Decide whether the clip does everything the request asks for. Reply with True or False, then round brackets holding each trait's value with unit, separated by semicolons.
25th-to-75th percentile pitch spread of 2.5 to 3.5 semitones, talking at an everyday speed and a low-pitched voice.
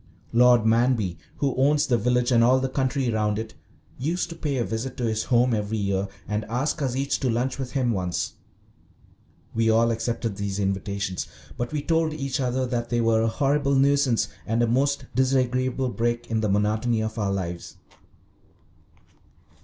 True (3.2 semitones; 175 wpm; 120 Hz)